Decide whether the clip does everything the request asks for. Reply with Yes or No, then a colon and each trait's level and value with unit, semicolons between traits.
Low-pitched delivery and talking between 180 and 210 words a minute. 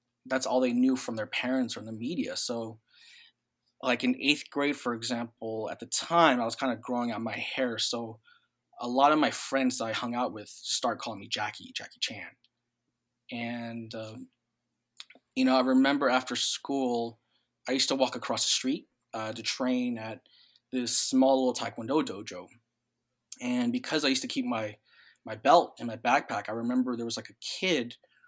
Yes: low, 120 Hz; average, 190 wpm